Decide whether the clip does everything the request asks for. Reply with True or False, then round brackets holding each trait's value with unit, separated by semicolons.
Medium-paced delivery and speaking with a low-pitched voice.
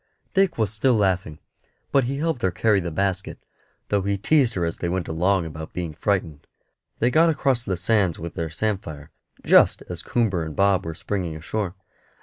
True (185 wpm; 95 Hz)